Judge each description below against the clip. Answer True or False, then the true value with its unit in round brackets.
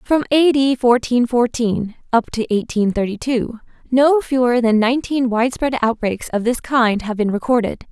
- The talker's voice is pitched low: False (240 Hz)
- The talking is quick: False (165 wpm)